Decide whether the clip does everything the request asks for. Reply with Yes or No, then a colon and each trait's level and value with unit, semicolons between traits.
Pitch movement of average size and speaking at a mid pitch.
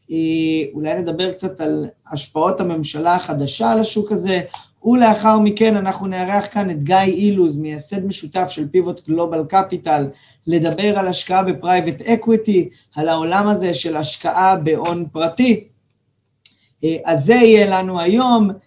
Yes: average, 3.9 semitones; medium, 180 Hz